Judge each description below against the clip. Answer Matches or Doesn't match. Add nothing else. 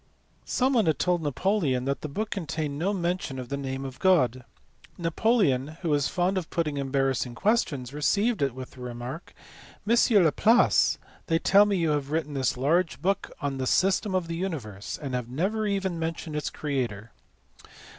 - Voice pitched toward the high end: Doesn't match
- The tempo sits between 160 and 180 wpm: Matches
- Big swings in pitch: Matches